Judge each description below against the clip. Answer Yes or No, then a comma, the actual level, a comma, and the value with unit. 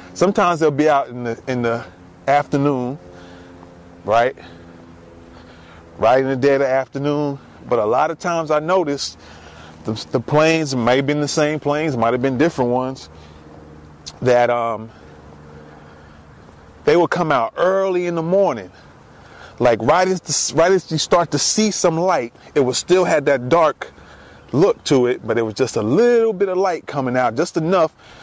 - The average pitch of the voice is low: Yes, low, 130 Hz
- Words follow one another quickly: No, average, 175 wpm